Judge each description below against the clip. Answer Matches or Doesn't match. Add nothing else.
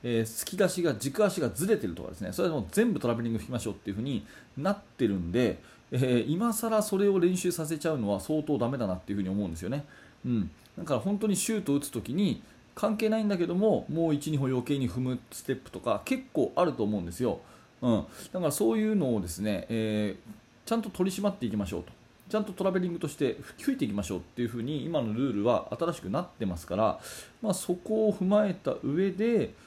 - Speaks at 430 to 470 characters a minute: Matches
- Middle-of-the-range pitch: Matches